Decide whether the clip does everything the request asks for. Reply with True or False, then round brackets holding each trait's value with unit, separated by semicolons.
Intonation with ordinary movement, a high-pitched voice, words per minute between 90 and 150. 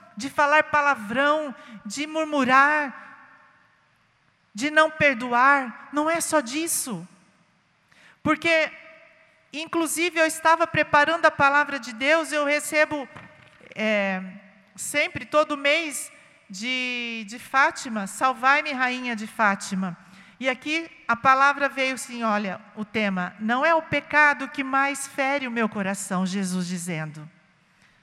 False (5.9 semitones; 275 Hz; 120 wpm)